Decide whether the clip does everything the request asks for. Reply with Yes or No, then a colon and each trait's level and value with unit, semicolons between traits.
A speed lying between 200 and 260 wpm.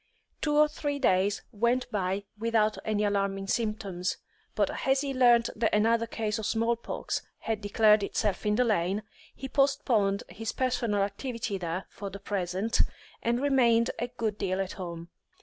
No: average, 165 wpm